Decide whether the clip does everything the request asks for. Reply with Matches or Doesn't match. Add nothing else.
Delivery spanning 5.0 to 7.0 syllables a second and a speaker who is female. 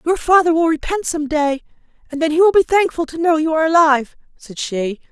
Matches